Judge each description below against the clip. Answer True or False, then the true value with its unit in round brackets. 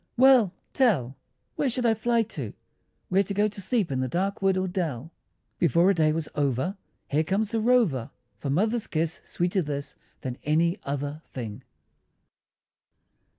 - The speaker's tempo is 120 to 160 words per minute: True (155 wpm)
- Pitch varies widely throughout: True (6.5 semitones)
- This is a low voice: False (175 Hz)